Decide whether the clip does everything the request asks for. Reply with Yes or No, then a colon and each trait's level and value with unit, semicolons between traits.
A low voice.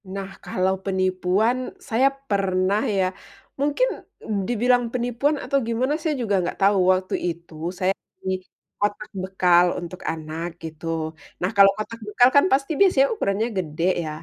No: high, 200 Hz